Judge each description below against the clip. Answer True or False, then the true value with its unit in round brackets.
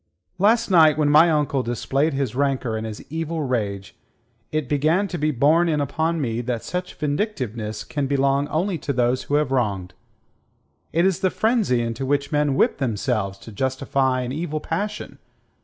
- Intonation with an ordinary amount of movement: True (4.5 semitones)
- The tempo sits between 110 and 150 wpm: False (175 wpm)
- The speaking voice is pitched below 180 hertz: True (140 Hz)